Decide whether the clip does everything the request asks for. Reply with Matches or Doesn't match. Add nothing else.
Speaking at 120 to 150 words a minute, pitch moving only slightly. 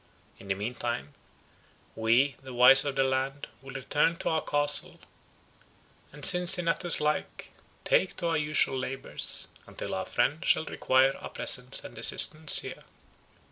Doesn't match